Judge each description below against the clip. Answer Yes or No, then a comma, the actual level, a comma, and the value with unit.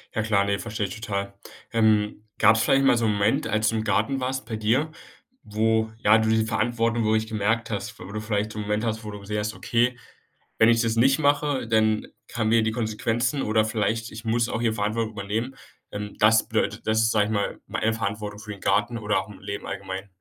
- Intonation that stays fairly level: Yes, narrow, 1.6 semitones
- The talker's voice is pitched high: No, low, 110 Hz